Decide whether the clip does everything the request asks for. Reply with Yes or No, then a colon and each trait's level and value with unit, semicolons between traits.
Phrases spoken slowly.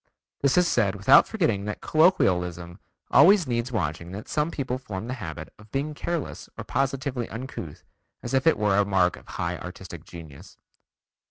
No: average, 175 wpm